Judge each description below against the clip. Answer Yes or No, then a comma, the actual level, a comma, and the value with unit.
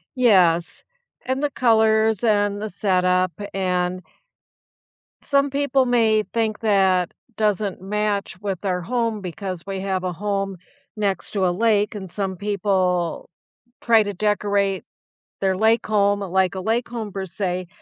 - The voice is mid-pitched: No, high, 200 Hz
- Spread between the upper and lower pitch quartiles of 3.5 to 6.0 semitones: No, average, 2.7 semitones